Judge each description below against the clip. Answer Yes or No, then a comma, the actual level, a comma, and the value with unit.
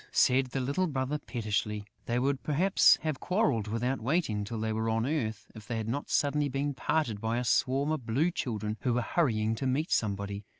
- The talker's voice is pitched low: Yes, low, 125 Hz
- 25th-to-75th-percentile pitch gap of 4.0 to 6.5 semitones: Yes, average, 4.5 semitones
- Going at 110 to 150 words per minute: No, fast, 205 wpm